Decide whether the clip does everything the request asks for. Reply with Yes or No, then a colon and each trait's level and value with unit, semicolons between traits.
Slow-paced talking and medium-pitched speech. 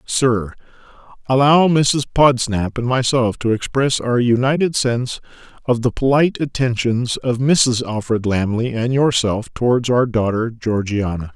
No: slow, 130 wpm; low, 120 Hz